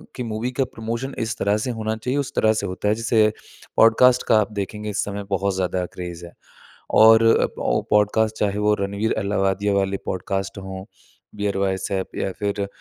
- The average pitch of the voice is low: Yes, low, 105 Hz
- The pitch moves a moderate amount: No, narrow, 2.2 semitones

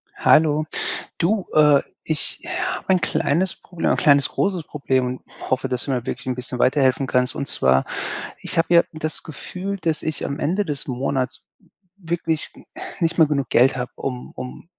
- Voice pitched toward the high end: No, medium, 145 Hz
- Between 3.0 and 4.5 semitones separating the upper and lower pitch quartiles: Yes, average, 4.2 semitones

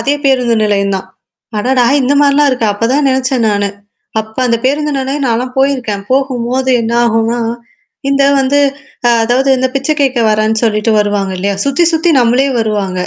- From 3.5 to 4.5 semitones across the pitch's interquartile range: Yes, average, 3.8 semitones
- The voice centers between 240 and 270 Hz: Yes, very high, 250 Hz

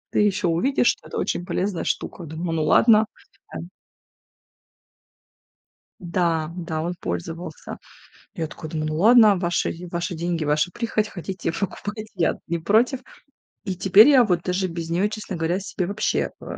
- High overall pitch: No, medium, 180 Hz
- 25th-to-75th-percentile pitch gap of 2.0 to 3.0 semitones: No, average, 3.8 semitones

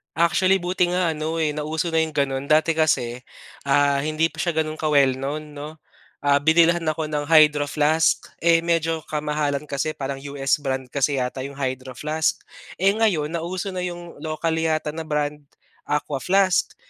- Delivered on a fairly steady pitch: Yes, narrow, 2.3 semitones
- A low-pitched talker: No, medium, 155 Hz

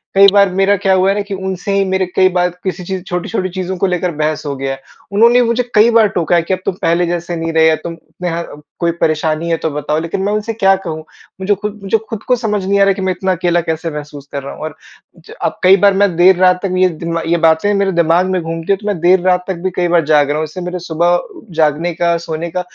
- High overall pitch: No, medium, 180 Hz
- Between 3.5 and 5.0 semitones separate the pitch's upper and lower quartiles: No, average, 2.7 semitones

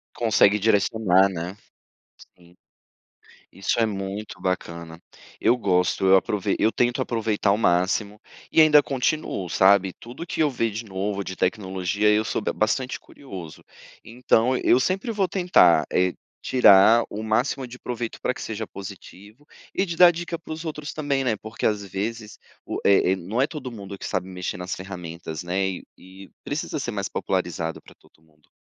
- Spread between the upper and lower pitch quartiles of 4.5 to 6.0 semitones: Yes, average, 4.8 semitones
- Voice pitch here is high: No, low, 105 Hz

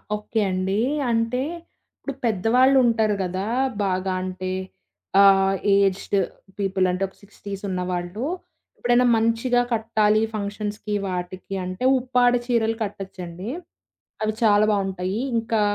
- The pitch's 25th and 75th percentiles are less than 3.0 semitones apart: No, average, 3.3 semitones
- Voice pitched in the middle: No, high, 205 Hz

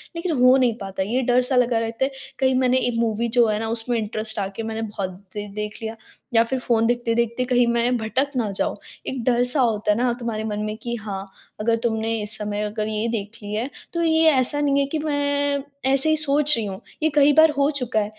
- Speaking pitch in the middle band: No, high, 235 Hz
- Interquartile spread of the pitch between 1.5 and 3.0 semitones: No, average, 3.5 semitones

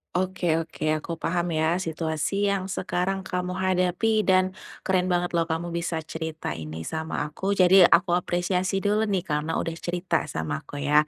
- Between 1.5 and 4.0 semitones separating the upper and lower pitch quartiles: Yes, narrow, 2.6 semitones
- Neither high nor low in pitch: Yes, medium, 175 Hz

